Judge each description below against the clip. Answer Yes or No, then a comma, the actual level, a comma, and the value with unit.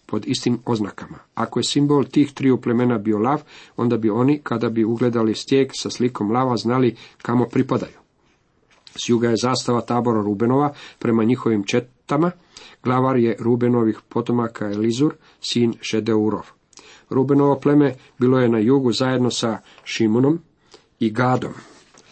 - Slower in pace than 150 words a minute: Yes, average, 140 wpm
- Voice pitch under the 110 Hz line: No, low, 120 Hz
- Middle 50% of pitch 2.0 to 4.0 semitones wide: Yes, narrow, 2.5 semitones